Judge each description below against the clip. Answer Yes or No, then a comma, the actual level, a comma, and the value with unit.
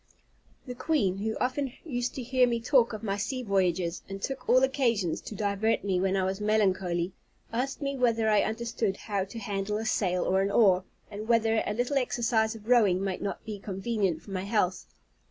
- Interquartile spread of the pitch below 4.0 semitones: Yes, average, 3.6 semitones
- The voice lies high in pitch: Yes, high, 215 Hz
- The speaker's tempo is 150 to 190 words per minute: No, average, 200 wpm